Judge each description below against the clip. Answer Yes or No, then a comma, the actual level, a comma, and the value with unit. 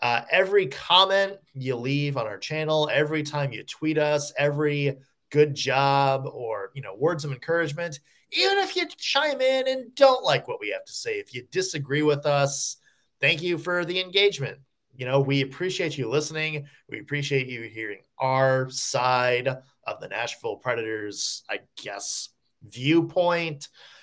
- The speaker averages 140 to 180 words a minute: Yes, average, 160 wpm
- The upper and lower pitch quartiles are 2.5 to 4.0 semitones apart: No, average, 4.5 semitones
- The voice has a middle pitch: Yes, medium, 145 Hz